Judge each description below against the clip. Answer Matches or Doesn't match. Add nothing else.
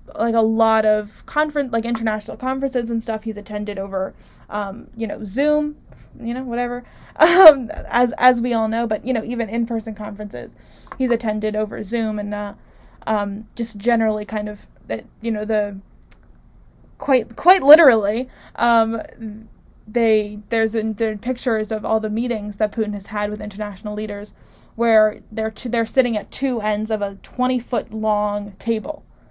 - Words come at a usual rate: Matches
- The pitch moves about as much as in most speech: Doesn't match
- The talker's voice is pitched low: Doesn't match